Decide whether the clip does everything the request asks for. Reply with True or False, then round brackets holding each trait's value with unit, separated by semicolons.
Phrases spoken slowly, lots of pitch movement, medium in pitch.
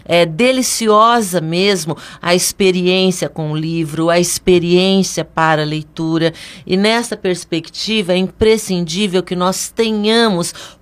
False (115 wpm; 3.8 semitones; 180 Hz)